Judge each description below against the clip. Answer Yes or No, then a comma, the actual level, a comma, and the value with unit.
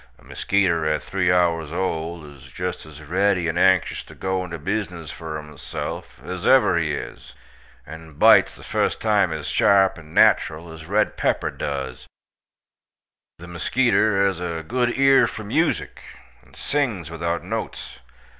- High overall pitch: No, very low, 85 Hz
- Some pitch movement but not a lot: Yes, average, 3.5 semitones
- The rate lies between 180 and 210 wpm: No, average, 155 wpm